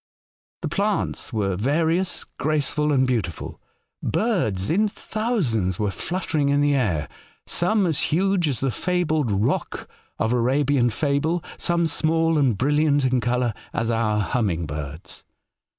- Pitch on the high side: No, medium, 140 Hz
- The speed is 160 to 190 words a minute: No, average, 145 wpm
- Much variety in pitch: Yes, wide, 6.4 semitones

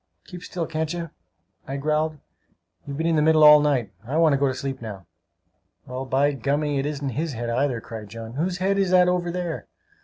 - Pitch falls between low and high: Yes, medium, 150 Hz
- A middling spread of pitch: Yes, average, 3.9 semitones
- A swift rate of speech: Yes, fast, 215 wpm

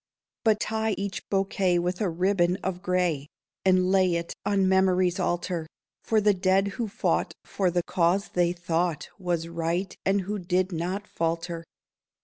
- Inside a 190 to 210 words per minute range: No, average, 155 wpm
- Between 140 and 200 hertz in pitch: Yes, medium, 185 Hz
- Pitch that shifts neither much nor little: No, narrow, 2.1 semitones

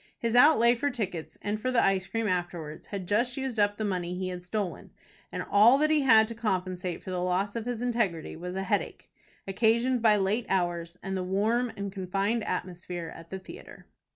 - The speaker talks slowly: No, fast, 205 wpm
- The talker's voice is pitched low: No, high, 200 Hz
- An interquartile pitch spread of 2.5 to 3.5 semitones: No, average, 4.3 semitones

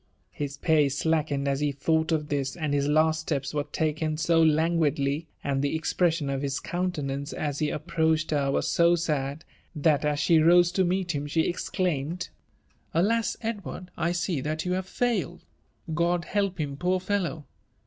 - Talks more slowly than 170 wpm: No, average, 190 wpm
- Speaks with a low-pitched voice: No, medium, 160 Hz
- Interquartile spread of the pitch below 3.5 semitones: Yes, average, 3.1 semitones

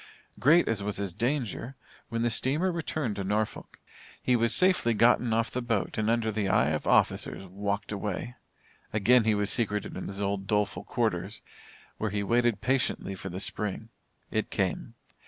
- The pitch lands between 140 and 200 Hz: No, low, 110 Hz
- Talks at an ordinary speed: Yes, average, 175 wpm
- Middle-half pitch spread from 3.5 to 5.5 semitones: No, average, 3.0 semitones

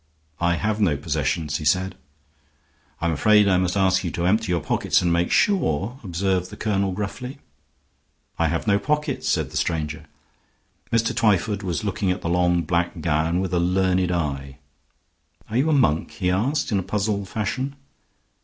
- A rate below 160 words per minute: No, average, 175 wpm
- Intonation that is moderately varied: Yes, average, 3.6 semitones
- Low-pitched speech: Yes, very low, 90 Hz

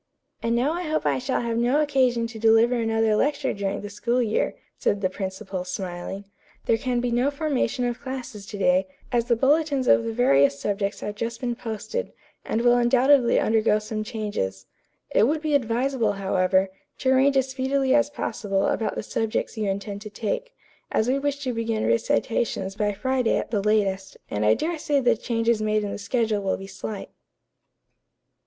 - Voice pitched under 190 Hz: No, high, 230 Hz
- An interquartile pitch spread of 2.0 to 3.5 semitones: No, average, 4.2 semitones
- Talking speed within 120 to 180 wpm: No, average, 190 wpm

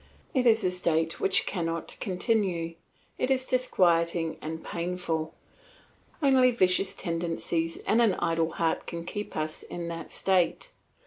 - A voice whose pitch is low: No, medium, 175 Hz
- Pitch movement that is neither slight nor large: Yes, average, 3.8 semitones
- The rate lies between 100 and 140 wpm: Yes, slow, 135 wpm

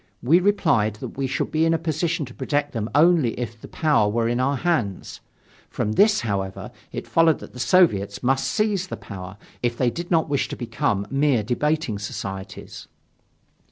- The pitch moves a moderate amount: No, wide, 6.9 semitones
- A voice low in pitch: Yes, low, 130 Hz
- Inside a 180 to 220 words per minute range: Yes, average, 185 wpm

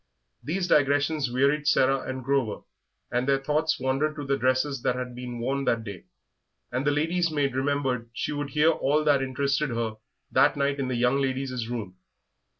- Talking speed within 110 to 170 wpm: No, average, 180 wpm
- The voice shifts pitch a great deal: No, narrow, 2.5 semitones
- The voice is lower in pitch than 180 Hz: Yes, low, 135 Hz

